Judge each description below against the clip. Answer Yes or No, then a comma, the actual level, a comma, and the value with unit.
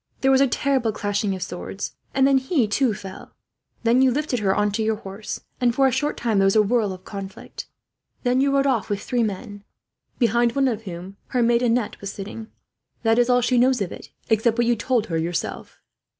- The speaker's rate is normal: No, fast, 220 wpm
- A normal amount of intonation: Yes, average, 3.8 semitones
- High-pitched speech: Yes, high, 230 Hz